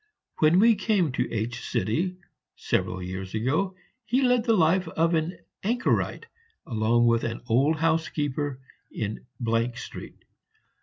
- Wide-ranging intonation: Yes, wide, 8.1 semitones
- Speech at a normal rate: No, slow, 120 wpm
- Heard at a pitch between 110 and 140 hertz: No, medium, 155 Hz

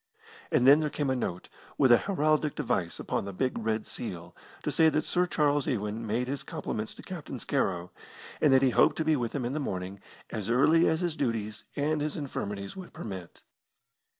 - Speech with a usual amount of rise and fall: No, wide, 6.0 semitones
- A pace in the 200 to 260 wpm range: Yes, fast, 205 wpm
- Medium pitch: No, low, 130 Hz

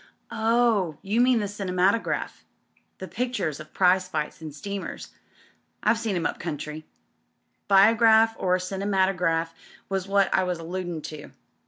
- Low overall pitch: No, high, 190 Hz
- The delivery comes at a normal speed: Yes, average, 145 wpm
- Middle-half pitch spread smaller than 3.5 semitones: No, average, 3.8 semitones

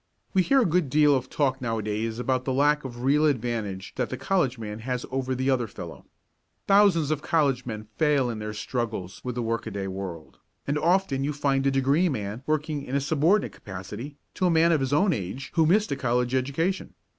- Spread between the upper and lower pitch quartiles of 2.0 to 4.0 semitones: No, average, 4.7 semitones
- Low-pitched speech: Yes, low, 130 Hz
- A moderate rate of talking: No, fast, 215 wpm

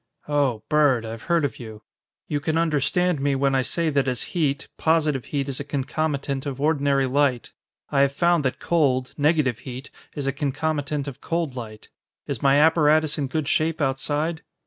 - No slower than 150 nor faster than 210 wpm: Yes, average, 180 wpm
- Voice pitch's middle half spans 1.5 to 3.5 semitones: Yes, average, 2.7 semitones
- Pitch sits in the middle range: Yes, medium, 145 Hz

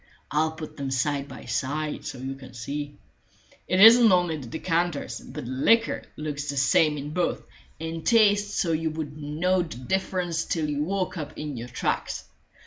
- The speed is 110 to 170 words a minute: No, average, 180 wpm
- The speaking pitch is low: No, medium, 155 Hz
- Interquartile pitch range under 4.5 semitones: Yes, average, 3.8 semitones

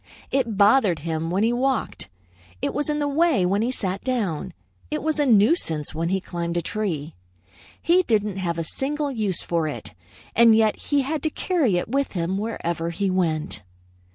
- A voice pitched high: Yes, high, 205 Hz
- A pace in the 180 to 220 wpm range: Yes, average, 185 wpm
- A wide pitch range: Yes, wide, 7.8 semitones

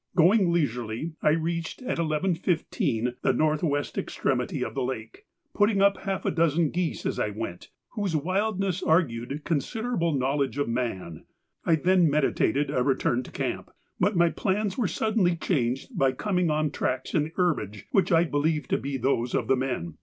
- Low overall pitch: No, medium, 155 Hz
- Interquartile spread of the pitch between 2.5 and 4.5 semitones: No, wide, 5.4 semitones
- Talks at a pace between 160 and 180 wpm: Yes, average, 175 wpm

